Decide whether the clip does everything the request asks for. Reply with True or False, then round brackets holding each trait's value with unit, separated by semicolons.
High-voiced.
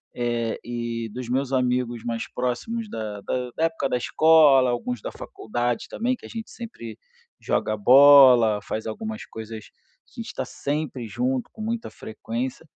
False (125 Hz)